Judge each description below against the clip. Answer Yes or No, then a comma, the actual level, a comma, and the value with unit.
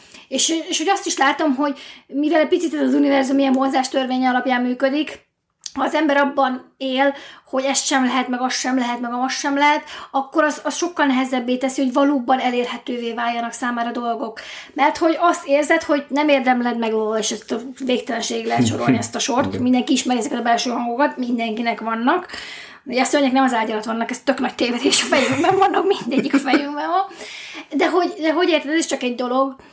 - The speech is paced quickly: Yes, fast, 195 wpm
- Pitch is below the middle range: No, very high, 270 Hz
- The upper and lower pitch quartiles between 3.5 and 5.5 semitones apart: No, average, 3.0 semitones